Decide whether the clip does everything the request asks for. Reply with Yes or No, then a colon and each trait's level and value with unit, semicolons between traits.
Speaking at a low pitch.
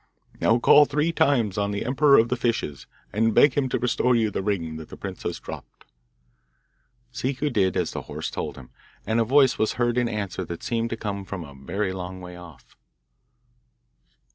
Yes: low, 110 Hz